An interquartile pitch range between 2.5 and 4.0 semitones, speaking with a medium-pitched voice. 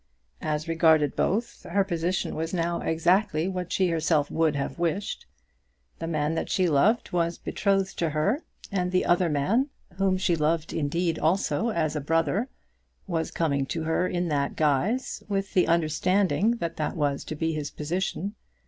Yes: average, 3.3 semitones; medium, 170 Hz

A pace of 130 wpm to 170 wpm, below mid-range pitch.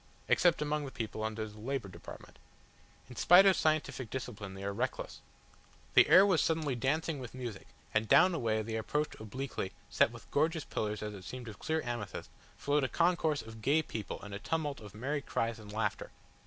No: average, 200 wpm; low, 125 Hz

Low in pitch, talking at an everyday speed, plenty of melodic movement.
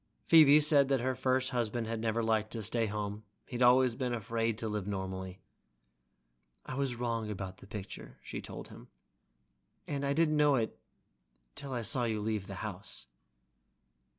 No: low, 115 Hz; average, 165 wpm; average, 3.5 semitones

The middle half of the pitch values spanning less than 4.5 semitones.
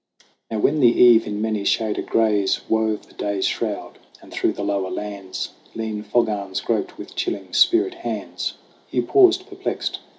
Yes: average, 3.0 semitones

